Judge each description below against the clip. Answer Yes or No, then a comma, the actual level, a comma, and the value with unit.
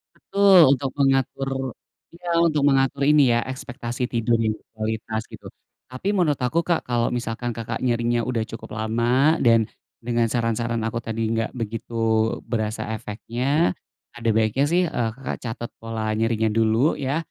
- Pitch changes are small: No, average, 3.2 semitones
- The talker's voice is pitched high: No, low, 120 Hz